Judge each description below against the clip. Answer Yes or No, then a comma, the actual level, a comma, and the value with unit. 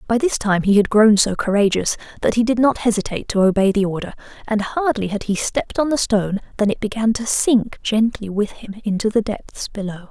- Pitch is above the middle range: Yes, high, 215 Hz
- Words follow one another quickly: Yes, fast, 220 wpm